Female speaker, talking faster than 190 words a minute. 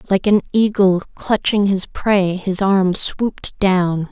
No: female; average, 145 wpm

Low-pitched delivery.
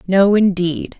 No: medium, 185 Hz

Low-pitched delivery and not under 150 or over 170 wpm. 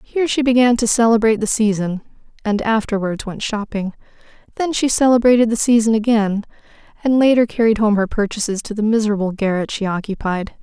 No: high, 220 Hz; average, 165 wpm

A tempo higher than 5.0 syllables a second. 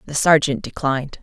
Yes: 5.7 syllables/s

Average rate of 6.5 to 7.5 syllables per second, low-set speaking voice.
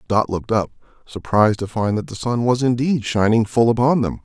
No: 5.7 syllables/s; low, 115 Hz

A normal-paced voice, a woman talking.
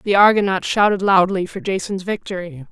Yes: average, 155 wpm; female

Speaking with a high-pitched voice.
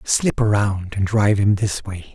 No: low, 105 Hz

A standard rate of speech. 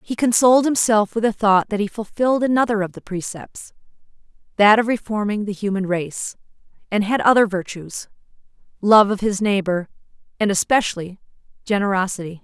No: slow, 130 wpm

